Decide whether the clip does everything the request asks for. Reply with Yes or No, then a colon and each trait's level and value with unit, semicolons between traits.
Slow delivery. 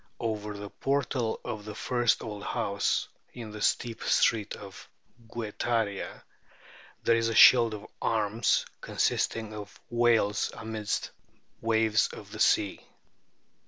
Yes: slow, 125 wpm